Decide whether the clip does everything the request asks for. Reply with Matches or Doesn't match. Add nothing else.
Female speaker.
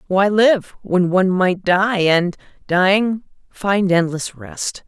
Matches